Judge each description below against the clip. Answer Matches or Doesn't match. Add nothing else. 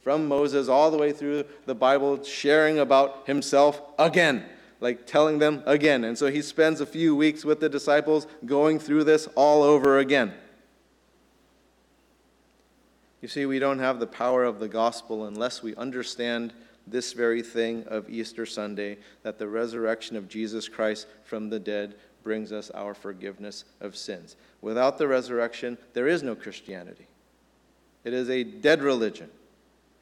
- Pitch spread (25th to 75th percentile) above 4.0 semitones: Matches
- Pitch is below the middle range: Matches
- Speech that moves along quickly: Doesn't match